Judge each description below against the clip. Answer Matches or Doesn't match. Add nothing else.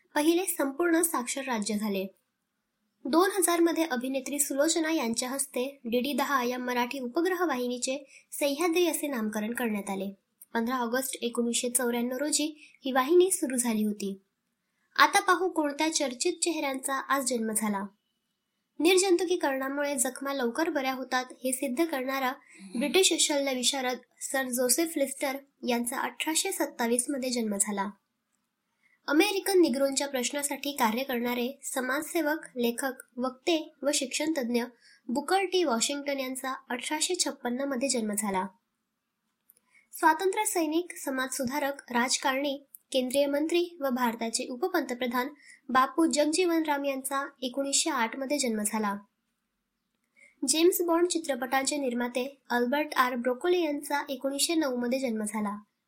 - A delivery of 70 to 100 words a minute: Doesn't match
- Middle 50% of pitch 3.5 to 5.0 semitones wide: Matches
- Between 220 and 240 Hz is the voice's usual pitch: Doesn't match